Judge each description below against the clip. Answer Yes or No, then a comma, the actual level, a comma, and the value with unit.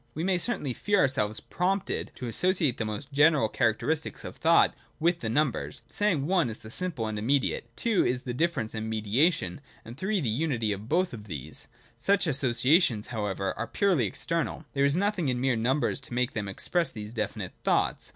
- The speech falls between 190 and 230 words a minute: Yes, average, 195 wpm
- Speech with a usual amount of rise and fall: No, wide, 7.1 semitones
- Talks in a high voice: No, low, 135 Hz